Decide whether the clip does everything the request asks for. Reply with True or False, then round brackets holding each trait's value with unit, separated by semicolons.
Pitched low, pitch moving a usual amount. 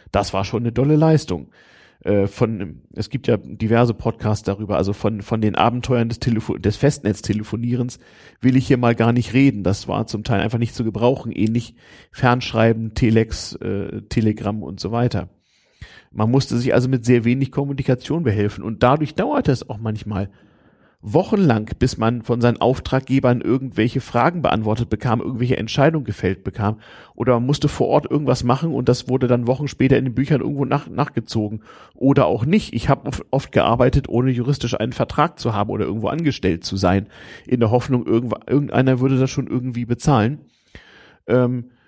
True (120 Hz; 3.5 semitones)